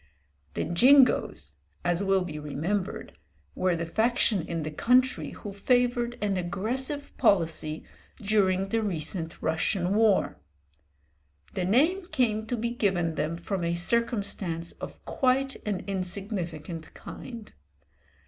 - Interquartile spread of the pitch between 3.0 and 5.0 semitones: No, wide, 5.5 semitones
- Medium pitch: No, high, 195 Hz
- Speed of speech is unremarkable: No, slow, 120 wpm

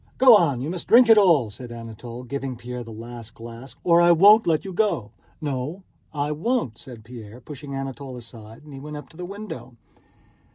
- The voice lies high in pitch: No, low, 135 Hz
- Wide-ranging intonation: Yes, wide, 6.3 semitones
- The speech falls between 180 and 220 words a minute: Yes, average, 200 wpm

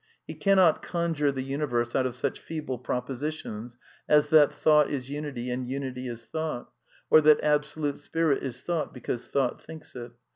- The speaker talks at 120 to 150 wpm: No, average, 175 wpm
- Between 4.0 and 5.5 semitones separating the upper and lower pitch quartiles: No, average, 3.6 semitones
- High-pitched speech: No, medium, 140 Hz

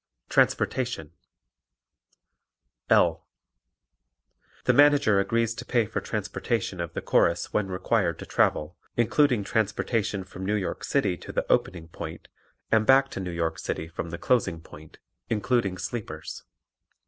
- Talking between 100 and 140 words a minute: Yes, slow, 135 wpm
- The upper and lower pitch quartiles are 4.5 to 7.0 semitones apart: Yes, average, 5.0 semitones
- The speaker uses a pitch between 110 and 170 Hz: No, low, 100 Hz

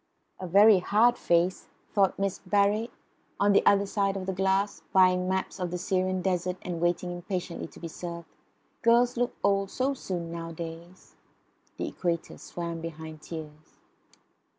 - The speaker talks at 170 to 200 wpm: No, average, 150 wpm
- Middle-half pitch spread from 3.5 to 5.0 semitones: No, average, 2.7 semitones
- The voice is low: No, medium, 185 Hz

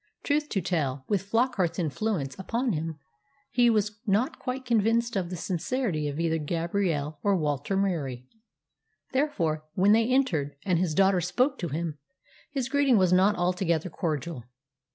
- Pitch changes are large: Yes, wide, 6.2 semitones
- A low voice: No, medium, 185 Hz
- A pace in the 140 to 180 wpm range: Yes, average, 155 wpm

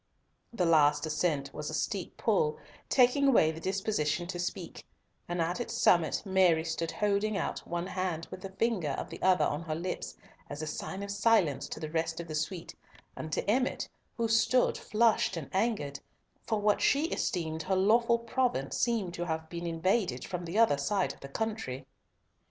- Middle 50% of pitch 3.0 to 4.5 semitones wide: No, average, 5.1 semitones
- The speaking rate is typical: Yes, average, 190 wpm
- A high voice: No, medium, 180 Hz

